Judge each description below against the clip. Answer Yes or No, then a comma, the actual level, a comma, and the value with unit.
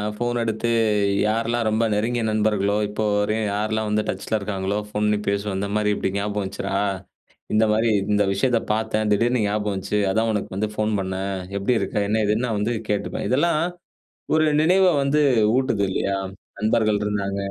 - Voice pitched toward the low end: Yes, low, 105 Hz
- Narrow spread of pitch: Yes, narrow, 1.8 semitones